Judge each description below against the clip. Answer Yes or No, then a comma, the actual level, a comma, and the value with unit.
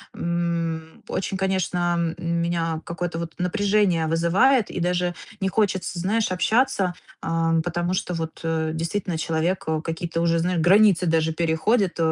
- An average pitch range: No, narrow, 2.3 semitones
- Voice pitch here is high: No, medium, 170 Hz